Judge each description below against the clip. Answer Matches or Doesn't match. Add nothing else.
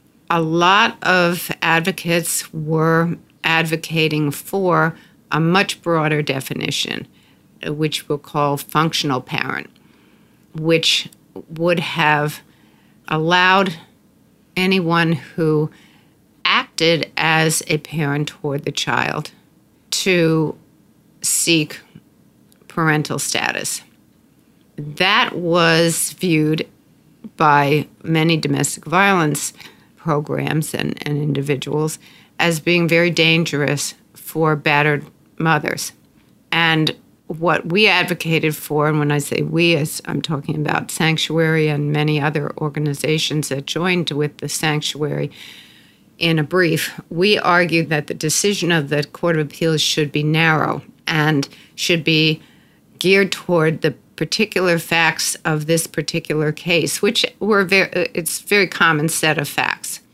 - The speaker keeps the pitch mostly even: Matches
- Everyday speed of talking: Doesn't match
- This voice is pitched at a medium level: Matches